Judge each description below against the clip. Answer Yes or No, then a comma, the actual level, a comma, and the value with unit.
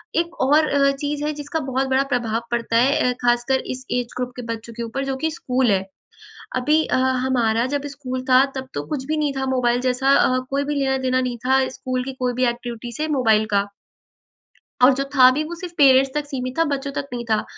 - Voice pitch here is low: No, very high, 260 Hz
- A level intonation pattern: Yes, narrow, 2.3 semitones